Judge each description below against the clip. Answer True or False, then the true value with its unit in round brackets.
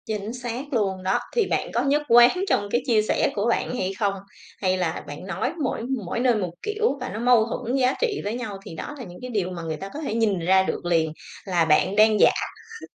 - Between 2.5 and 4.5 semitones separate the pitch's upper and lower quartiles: False (5.0 semitones)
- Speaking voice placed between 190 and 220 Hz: True (215 Hz)